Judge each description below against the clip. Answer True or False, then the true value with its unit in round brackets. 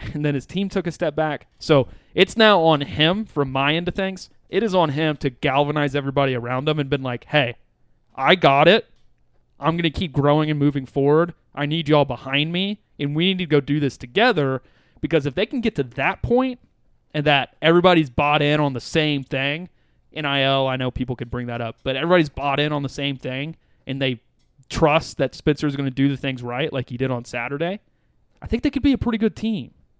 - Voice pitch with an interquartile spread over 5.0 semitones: False (3.5 semitones)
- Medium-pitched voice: True (145 Hz)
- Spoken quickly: True (230 wpm)